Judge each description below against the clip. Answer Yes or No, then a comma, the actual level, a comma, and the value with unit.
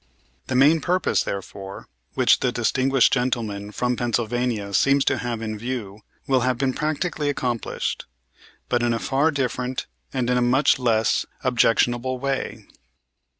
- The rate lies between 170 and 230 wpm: No, average, 145 wpm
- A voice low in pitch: Yes, low, 125 Hz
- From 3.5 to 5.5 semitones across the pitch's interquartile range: No, narrow, 2.6 semitones